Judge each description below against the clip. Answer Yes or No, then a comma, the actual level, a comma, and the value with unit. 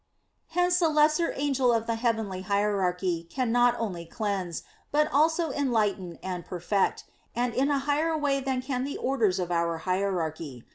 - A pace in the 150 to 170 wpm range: Yes, average, 160 wpm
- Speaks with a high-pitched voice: Yes, high, 230 Hz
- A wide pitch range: Yes, wide, 7.2 semitones